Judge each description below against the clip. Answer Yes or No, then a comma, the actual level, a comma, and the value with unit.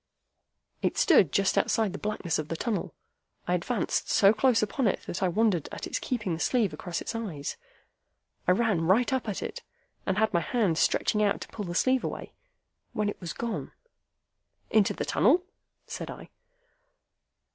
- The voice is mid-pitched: No, high, 205 Hz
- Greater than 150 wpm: Yes, average, 180 wpm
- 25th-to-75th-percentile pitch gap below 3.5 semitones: No, average, 4.4 semitones